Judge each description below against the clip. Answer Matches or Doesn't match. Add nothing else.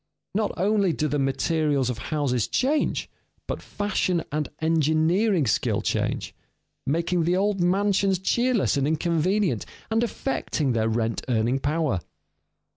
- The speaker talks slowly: Matches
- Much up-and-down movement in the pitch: Matches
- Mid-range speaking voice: Matches